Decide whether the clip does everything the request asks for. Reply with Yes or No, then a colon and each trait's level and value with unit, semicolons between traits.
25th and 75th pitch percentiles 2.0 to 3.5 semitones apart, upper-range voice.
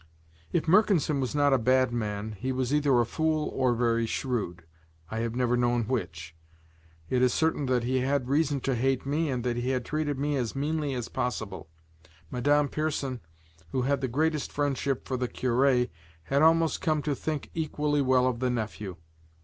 No: average, 3.2 semitones; low, 130 Hz